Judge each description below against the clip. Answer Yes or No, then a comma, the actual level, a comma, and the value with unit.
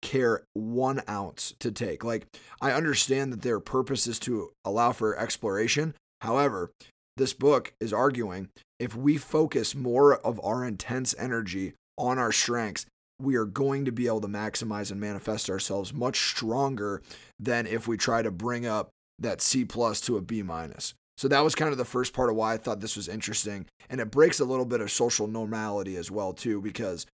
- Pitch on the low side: Yes, low, 115 Hz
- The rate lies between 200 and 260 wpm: No, average, 190 wpm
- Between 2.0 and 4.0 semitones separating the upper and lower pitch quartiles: Yes, average, 3.6 semitones